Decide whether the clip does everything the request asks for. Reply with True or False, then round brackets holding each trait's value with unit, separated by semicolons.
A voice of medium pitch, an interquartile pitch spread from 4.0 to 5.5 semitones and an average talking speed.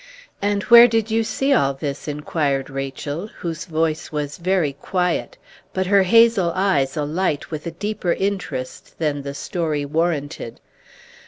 True (165 Hz; 5.1 semitones; 145 wpm)